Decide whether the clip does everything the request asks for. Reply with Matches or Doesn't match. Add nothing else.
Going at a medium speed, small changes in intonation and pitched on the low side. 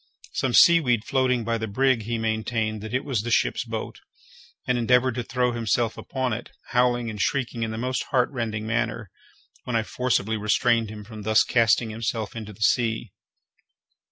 Matches